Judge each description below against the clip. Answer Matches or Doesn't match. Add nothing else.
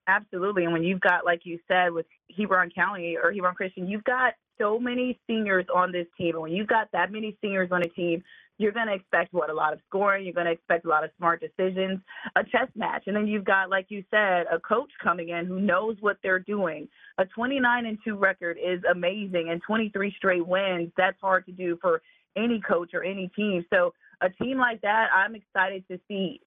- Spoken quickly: Matches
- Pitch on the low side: Doesn't match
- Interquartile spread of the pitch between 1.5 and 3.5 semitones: Matches